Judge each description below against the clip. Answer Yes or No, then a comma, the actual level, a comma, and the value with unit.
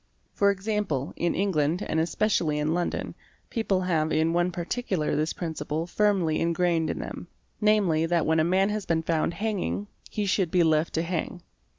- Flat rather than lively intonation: No, average, 3.4 semitones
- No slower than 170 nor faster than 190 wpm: Yes, average, 175 wpm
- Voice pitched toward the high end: No, medium, 170 Hz